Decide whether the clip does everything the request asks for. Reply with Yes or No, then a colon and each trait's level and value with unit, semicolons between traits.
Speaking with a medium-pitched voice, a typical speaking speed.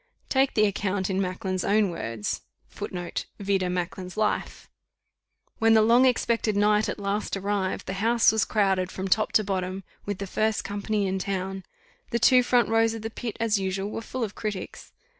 No: high, 205 Hz; average, 180 wpm